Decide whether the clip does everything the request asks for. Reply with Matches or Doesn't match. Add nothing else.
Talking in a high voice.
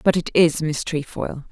Doesn't match